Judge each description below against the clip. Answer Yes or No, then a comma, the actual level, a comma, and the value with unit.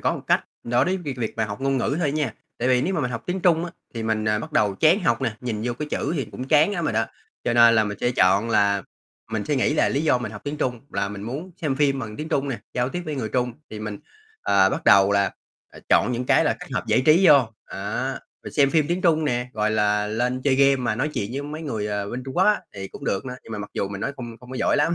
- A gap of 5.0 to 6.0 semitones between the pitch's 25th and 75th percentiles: Yes, average, 5.3 semitones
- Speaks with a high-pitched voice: No, low, 125 Hz